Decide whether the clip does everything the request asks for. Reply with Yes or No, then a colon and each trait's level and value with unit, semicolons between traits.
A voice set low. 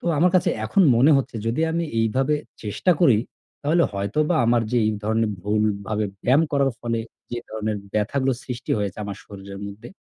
Yes: low, 115 Hz